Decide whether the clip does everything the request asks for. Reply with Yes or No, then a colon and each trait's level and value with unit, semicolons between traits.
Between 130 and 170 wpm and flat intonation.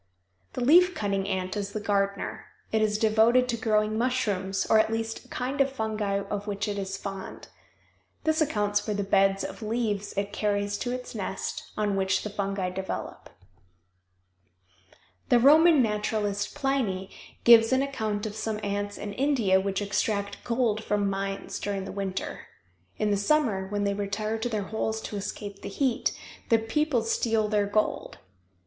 Yes: average, 165 wpm; narrow, 2.3 semitones